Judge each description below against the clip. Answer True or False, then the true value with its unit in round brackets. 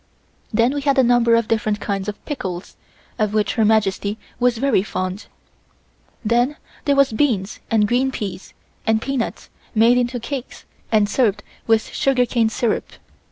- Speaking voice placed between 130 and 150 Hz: False (230 Hz)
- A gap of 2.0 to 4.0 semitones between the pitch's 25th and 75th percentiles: True (3.0 semitones)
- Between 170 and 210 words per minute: False (155 wpm)